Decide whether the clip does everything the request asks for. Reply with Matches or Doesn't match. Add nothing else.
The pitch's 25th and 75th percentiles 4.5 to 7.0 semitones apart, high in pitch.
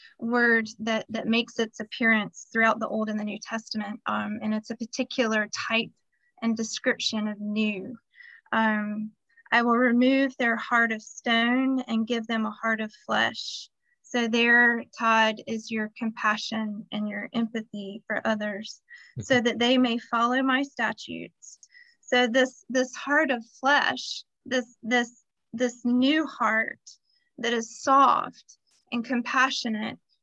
Doesn't match